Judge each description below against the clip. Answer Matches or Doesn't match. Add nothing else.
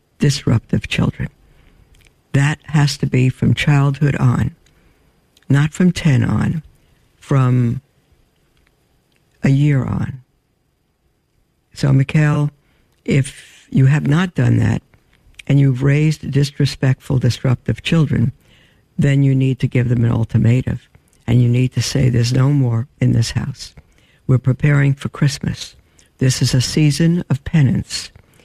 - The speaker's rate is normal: Doesn't match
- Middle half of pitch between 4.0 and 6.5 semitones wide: Doesn't match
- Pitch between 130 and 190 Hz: Matches